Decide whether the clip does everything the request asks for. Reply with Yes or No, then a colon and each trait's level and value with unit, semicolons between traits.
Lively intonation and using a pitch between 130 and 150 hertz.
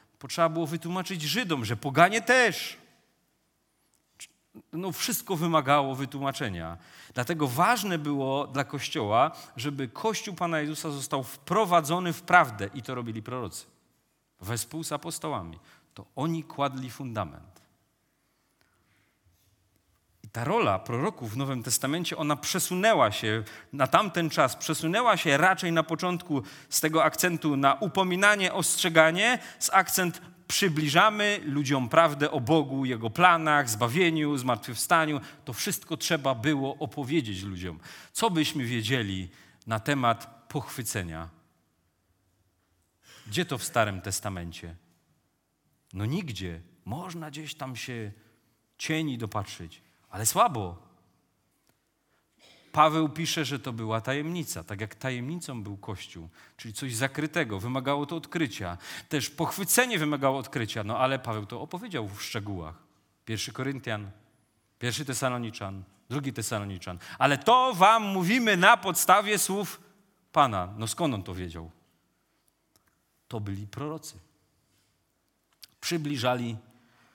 Yes: wide, 7.1 semitones; low, 135 Hz